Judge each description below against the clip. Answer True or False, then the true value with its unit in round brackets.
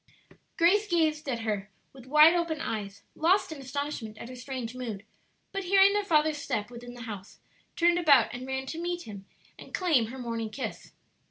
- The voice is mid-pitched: False (265 Hz)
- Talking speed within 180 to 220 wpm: True (185 wpm)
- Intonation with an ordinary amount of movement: False (6.6 semitones)